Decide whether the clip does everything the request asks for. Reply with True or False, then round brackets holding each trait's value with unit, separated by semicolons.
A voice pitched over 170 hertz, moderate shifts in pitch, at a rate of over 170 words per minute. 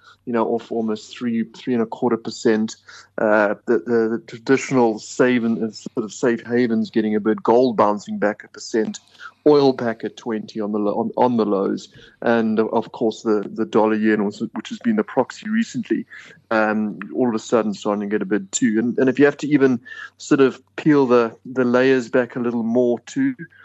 False (115 Hz; 3.2 semitones; 205 wpm)